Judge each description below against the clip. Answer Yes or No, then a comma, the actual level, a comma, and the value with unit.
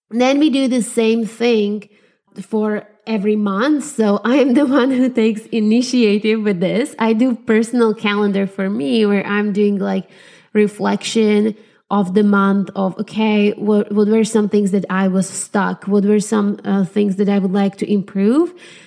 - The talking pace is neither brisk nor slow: Yes, average, 175 wpm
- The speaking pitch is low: No, high, 210 Hz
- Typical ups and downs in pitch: No, narrow, 1.9 semitones